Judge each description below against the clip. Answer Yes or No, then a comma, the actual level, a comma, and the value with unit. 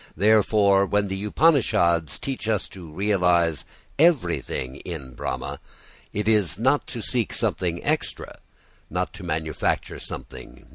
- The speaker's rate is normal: No, slow, 130 wpm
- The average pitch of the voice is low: Yes, very low, 95 Hz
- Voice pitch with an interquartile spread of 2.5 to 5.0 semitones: Yes, average, 4.3 semitones